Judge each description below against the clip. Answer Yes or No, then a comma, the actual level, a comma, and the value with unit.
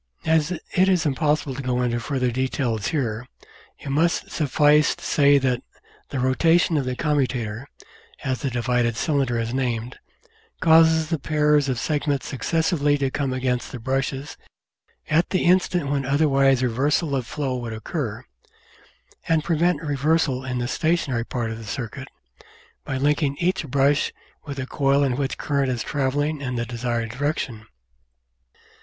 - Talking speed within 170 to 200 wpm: No, average, 155 wpm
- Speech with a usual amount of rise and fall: Yes, average, 3.2 semitones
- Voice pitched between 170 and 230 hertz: No, low, 135 Hz